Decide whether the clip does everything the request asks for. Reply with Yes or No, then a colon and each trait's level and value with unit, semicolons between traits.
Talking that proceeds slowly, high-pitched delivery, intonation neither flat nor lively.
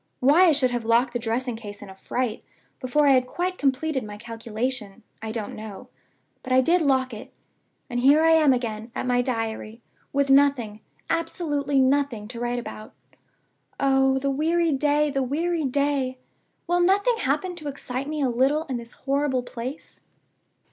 No: average, 175 wpm; very high, 265 Hz; average, 3.5 semitones